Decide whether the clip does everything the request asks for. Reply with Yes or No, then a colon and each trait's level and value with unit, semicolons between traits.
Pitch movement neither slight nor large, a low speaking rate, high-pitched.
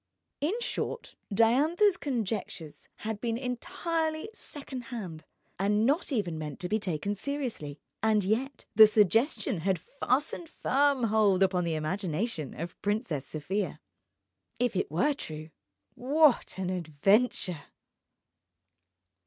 No: wide, 6.7 semitones; slow, 120 wpm; high, 215 Hz